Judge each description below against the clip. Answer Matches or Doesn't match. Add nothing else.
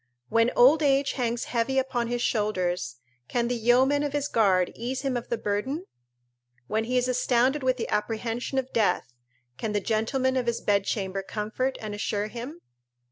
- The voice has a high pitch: Matches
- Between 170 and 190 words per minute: Matches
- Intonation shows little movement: Doesn't match